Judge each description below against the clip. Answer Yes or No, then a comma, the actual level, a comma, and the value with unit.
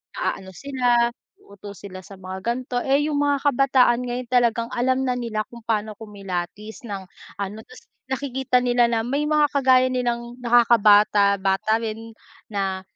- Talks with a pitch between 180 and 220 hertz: No, high, 235 Hz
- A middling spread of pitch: Yes, average, 3.5 semitones